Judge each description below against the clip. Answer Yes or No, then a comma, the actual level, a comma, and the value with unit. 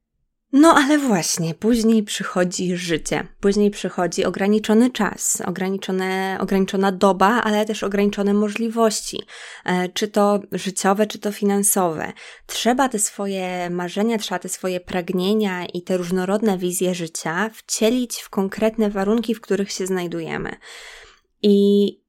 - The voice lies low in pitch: No, high, 200 Hz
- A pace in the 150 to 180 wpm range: No, average, 120 wpm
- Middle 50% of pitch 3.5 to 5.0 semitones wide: No, narrow, 2.6 semitones